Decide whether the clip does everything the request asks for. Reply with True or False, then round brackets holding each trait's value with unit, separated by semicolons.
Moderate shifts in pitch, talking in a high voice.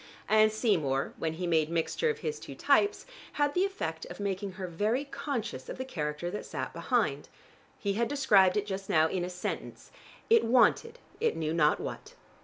False (7.8 semitones; 195 Hz)